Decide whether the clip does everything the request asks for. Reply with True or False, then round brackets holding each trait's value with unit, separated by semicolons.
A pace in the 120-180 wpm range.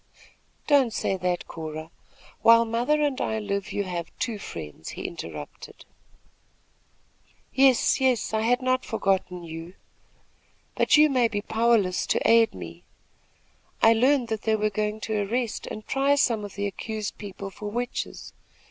True (150 wpm)